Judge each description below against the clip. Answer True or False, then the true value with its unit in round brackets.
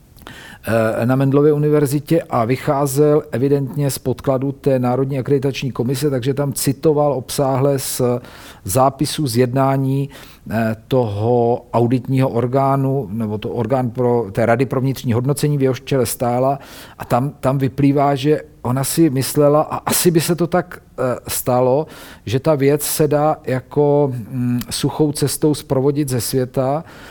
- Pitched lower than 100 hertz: False (135 Hz)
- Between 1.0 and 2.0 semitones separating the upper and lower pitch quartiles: False (2.6 semitones)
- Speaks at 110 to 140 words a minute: True (135 wpm)